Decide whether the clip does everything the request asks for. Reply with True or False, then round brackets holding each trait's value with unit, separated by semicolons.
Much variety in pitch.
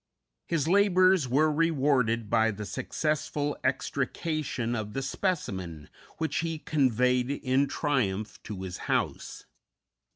True (5.8 semitones)